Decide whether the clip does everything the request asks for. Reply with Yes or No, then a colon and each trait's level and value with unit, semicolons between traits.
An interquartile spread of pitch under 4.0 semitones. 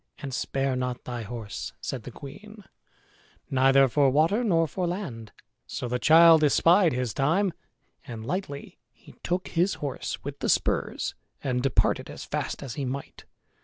No: average, 5.1 semitones